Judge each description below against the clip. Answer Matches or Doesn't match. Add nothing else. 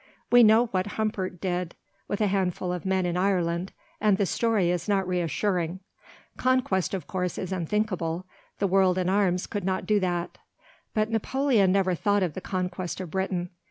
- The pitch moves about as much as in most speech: Doesn't match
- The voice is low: Doesn't match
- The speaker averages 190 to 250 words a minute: Doesn't match